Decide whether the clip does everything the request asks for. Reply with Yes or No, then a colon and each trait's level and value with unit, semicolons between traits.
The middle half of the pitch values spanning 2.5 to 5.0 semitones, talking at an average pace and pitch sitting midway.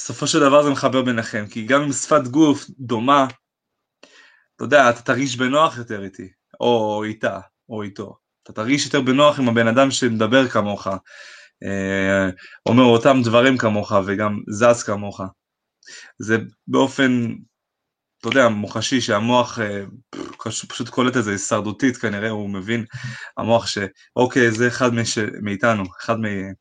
No: average, 3.7 semitones; average, 140 wpm; low, 115 Hz